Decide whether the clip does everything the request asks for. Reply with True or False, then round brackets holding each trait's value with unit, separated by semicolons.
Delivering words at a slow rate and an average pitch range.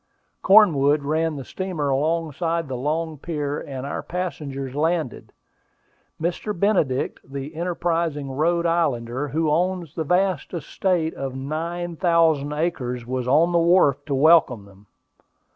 True (130 wpm; 3.7 semitones)